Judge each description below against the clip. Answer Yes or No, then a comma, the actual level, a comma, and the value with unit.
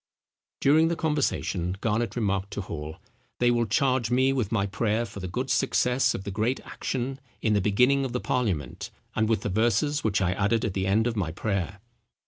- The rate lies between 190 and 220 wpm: Yes, average, 200 wpm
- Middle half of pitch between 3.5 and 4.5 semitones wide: Yes, average, 4.1 semitones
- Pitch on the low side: Yes, low, 110 Hz